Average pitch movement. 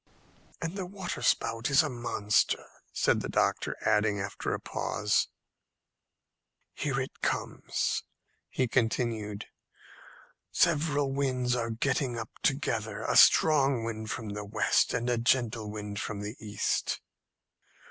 Yes: average, 4.2 semitones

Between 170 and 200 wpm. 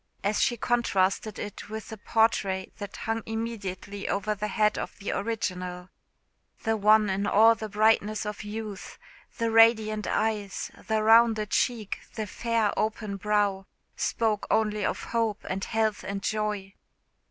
No: average, 145 wpm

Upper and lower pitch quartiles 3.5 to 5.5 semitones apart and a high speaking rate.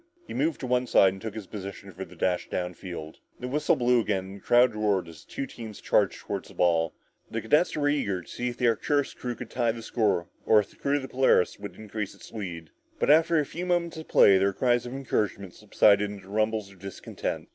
Yes: average, 4.5 semitones; fast, 245 wpm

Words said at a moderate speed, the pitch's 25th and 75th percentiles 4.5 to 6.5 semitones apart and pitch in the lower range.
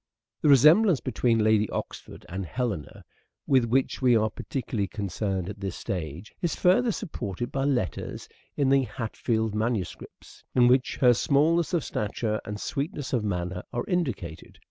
Yes: average, 160 wpm; average, 5.1 semitones; low, 120 Hz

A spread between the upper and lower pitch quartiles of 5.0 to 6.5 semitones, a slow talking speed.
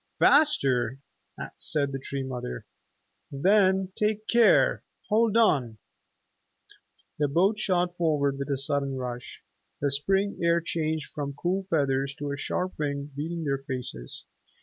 Yes: average, 5.3 semitones; slow, 130 wpm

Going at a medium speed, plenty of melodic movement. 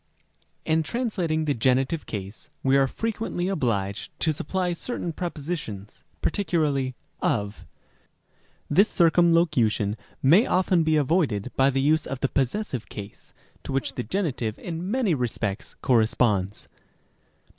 No: slow, 125 wpm; wide, 6.8 semitones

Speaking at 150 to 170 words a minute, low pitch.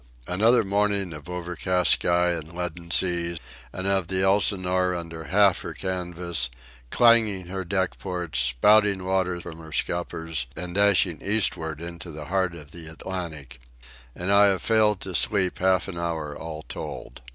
Yes: average, 155 wpm; very low, 90 Hz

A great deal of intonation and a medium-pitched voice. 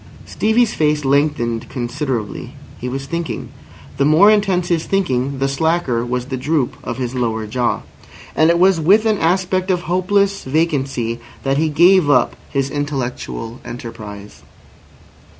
Yes: wide, 5.8 semitones; medium, 145 Hz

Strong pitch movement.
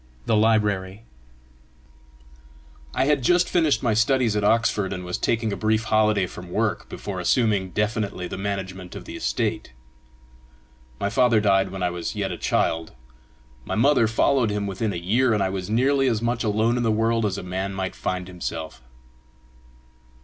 No: average, 3.4 semitones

